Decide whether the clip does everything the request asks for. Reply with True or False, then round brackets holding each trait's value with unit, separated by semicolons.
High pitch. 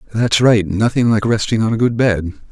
False (110 Hz)